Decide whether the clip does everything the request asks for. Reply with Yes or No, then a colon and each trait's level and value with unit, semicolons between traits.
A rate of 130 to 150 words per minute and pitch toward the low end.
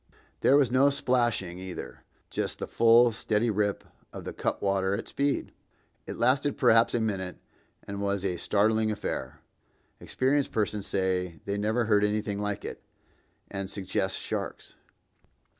Yes: average, 140 wpm; low, 105 Hz